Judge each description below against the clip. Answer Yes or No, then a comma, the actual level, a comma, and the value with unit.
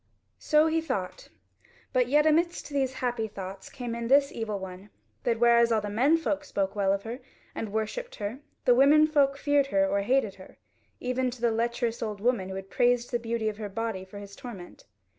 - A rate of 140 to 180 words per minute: No, fast, 205 wpm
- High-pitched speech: Yes, high, 235 Hz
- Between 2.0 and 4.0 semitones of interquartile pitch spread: No, average, 4.9 semitones